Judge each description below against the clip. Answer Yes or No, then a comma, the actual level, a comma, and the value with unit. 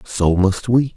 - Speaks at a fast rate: No, average, 190 wpm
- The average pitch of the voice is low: Yes, low, 100 Hz